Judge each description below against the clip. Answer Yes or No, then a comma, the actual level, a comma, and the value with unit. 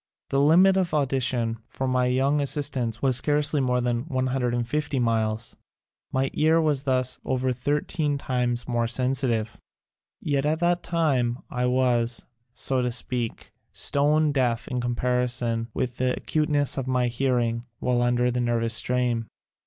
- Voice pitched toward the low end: Yes, low, 125 Hz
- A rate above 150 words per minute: No, average, 145 wpm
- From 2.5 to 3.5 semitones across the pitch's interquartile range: Yes, average, 2.8 semitones